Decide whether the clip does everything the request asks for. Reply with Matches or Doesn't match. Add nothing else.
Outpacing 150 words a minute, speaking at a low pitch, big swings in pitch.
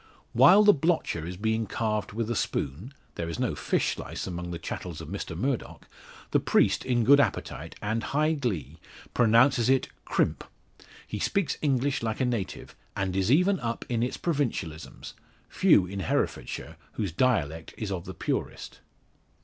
Matches